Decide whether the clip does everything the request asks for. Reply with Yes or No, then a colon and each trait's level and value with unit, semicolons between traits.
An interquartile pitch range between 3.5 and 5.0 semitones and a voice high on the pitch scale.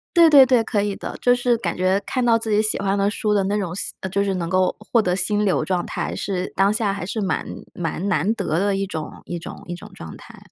No: average, 2.8 semitones; high, 200 Hz